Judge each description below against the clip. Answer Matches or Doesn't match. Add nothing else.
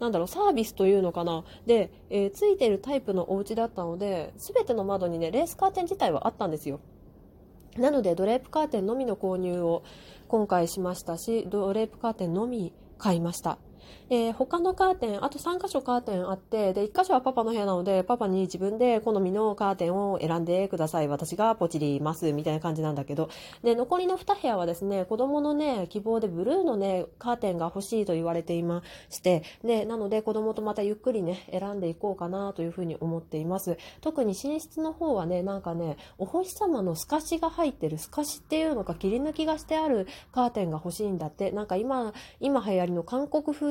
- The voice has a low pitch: Doesn't match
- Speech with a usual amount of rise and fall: Doesn't match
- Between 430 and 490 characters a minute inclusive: Doesn't match